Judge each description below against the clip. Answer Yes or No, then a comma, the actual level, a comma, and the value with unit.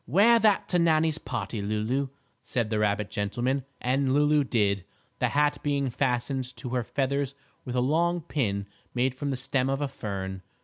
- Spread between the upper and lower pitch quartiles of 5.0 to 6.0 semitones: No, average, 4.0 semitones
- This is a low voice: Yes, low, 130 Hz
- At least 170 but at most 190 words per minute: Yes, average, 175 wpm